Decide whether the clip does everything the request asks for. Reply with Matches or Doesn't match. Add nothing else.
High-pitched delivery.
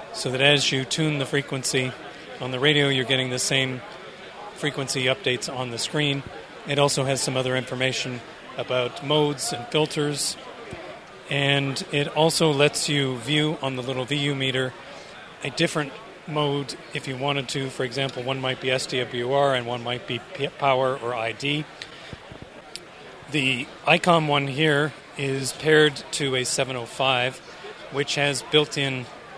Doesn't match